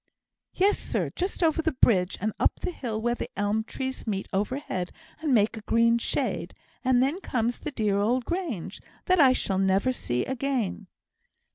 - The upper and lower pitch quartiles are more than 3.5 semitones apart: Yes, average, 5.0 semitones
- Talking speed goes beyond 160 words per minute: Yes, average, 175 wpm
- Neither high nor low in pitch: No, high, 235 Hz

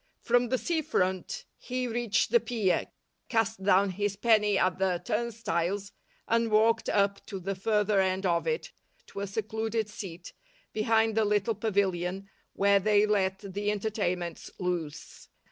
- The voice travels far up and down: No, average, 2.7 semitones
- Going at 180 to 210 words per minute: No, average, 145 wpm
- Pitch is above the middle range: Yes, high, 205 Hz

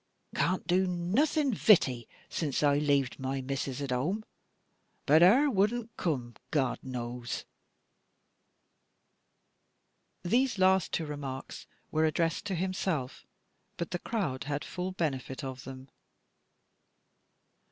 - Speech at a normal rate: No, slow, 110 wpm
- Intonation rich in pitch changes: Yes, wide, 6.0 semitones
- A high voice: No, medium, 155 Hz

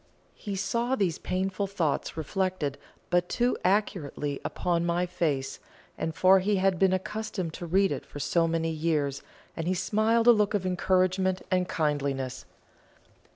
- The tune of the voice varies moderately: Yes, average, 3.2 semitones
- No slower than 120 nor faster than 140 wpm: No, average, 150 wpm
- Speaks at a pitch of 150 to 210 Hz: Yes, medium, 185 Hz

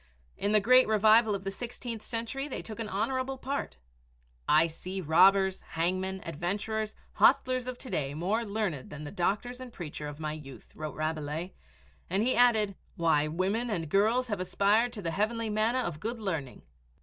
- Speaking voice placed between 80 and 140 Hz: No, high, 200 Hz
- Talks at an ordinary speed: Yes, average, 180 wpm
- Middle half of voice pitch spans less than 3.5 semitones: No, wide, 5.6 semitones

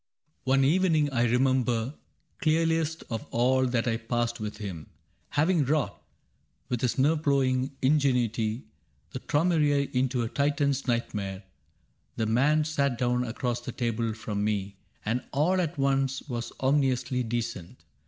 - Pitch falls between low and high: No, low, 130 Hz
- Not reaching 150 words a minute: Yes, average, 140 wpm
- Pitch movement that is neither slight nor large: Yes, average, 3.6 semitones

